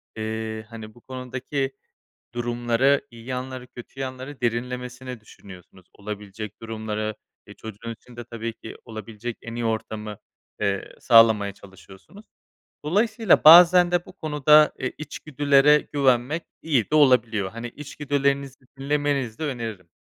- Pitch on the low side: Yes, low, 120 Hz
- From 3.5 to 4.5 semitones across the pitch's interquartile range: Yes, average, 4.1 semitones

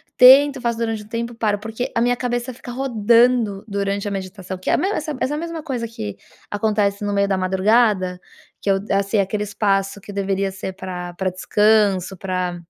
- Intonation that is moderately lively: Yes, average, 3.4 semitones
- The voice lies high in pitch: Yes, high, 205 Hz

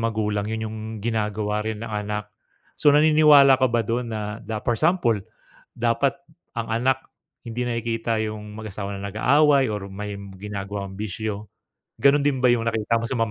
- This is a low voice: Yes, low, 110 Hz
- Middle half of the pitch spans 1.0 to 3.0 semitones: Yes, average, 2.7 semitones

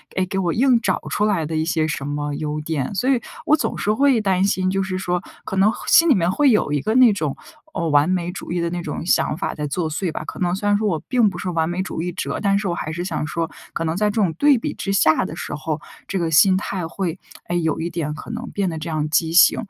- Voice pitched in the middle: Yes, medium, 180 Hz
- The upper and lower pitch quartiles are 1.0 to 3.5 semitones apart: No, average, 3.9 semitones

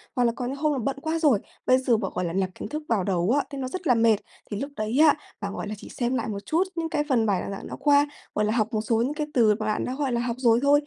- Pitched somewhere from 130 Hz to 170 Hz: No, high, 245 Hz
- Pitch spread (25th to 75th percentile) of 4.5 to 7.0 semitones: Yes, average, 4.9 semitones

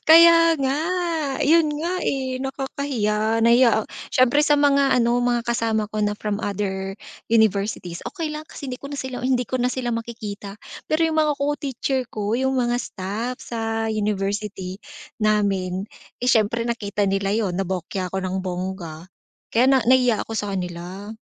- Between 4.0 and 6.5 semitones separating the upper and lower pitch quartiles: Yes, average, 4.7 semitones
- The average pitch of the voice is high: Yes, high, 225 Hz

